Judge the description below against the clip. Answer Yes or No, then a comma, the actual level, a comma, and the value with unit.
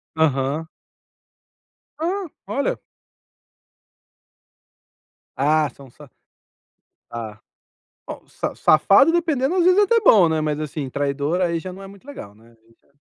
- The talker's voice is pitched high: No, medium, 160 Hz